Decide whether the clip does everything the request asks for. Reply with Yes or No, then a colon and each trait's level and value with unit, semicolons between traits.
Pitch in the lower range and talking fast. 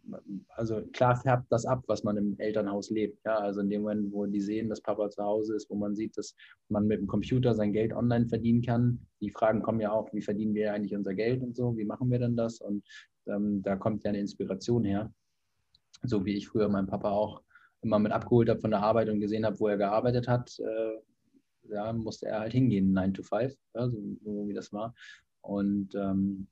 Yes: low, 105 Hz; fast, 230 wpm